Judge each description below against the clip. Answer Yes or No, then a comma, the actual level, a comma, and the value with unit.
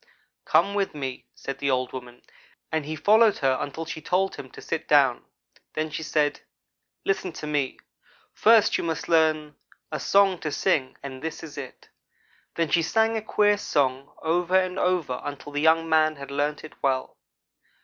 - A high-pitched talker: No, medium, 155 Hz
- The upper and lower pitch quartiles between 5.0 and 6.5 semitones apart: No, average, 4.3 semitones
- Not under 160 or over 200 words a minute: Yes, average, 180 wpm